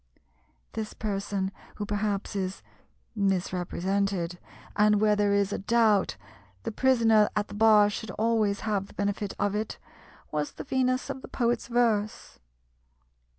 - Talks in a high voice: Yes, high, 210 Hz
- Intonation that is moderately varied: No, narrow, 1.9 semitones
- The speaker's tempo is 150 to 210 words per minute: No, average, 140 wpm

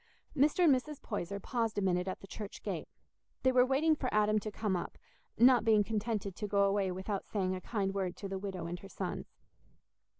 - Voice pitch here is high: Yes, high, 205 Hz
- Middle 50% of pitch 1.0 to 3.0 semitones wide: No, average, 3.6 semitones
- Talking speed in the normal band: No, fast, 210 wpm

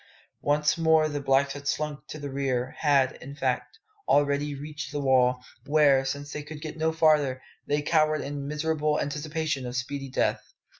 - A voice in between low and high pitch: Yes, medium, 145 Hz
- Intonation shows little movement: Yes, narrow, 1.9 semitones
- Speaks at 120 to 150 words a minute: No, average, 170 wpm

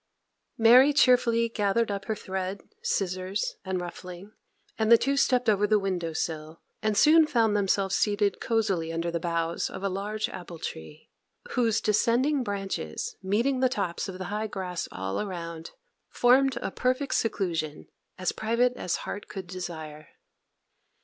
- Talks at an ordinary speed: Yes, average, 150 wpm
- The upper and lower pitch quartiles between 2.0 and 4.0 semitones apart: No, average, 4.6 semitones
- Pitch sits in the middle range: No, high, 200 Hz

